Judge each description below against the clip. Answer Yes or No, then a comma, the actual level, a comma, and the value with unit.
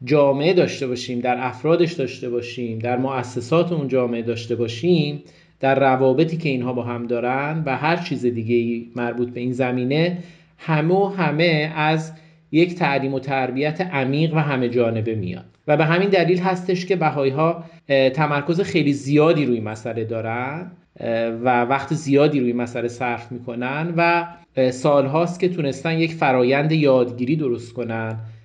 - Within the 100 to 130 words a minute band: No, average, 150 wpm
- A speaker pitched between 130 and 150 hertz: Yes, low, 135 Hz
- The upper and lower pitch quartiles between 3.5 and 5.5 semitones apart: Yes, average, 4.8 semitones